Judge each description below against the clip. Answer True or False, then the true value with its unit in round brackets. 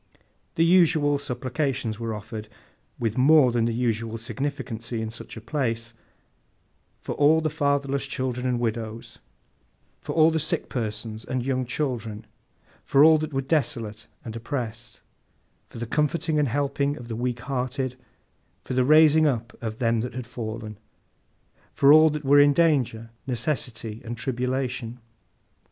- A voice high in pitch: False (125 Hz)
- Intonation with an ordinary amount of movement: True (3.9 semitones)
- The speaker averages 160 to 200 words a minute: False (145 wpm)